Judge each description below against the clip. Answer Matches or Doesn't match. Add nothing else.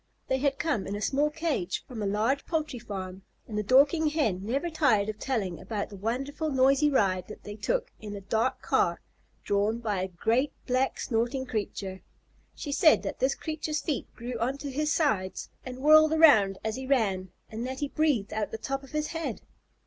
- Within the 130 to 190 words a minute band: Doesn't match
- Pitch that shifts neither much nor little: Doesn't match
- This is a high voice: Matches